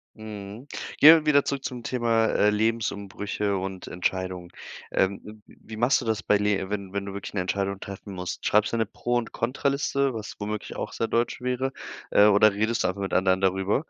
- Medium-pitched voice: No, low, 105 Hz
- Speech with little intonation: No, average, 3.1 semitones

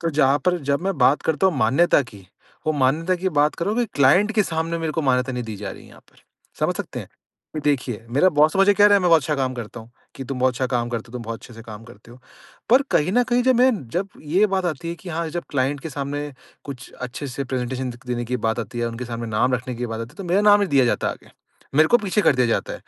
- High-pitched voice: No, medium, 140 Hz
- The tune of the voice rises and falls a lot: Yes, wide, 5.8 semitones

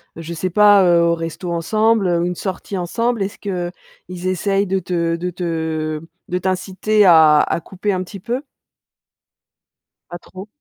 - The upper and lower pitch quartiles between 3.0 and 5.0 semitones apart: No, narrow, 2.6 semitones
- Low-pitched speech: No, medium, 180 Hz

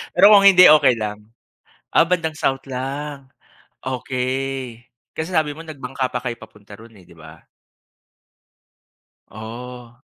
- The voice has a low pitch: Yes, low, 130 Hz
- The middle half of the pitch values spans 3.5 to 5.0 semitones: Yes, average, 4.2 semitones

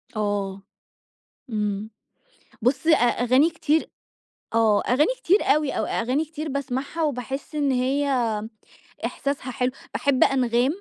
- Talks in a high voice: Yes, very high, 260 Hz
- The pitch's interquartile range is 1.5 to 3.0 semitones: No, average, 3.6 semitones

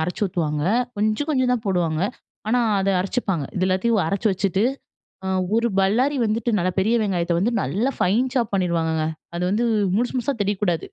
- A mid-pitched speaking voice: No, high, 195 Hz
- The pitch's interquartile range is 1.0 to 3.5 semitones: No, average, 4.6 semitones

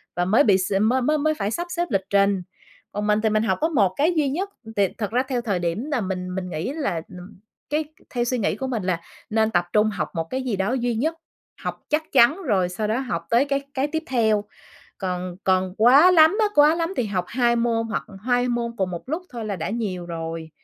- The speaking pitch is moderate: No, high, 225 Hz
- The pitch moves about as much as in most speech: No, wide, 5.8 semitones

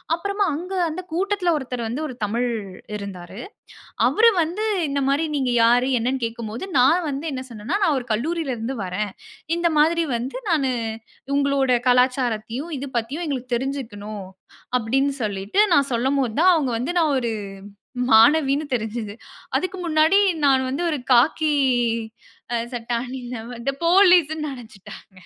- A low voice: No, very high, 265 Hz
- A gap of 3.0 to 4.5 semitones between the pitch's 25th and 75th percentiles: No, average, 5.1 semitones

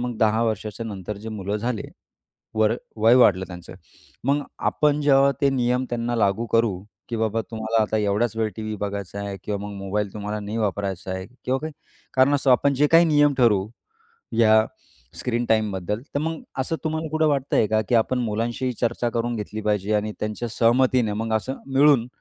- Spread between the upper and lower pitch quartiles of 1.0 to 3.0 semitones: No, average, 3.5 semitones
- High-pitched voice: No, low, 115 Hz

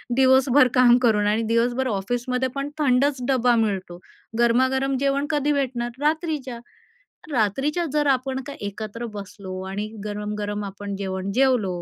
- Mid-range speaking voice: No, high, 245 Hz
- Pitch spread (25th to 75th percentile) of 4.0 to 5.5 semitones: Yes, average, 4.5 semitones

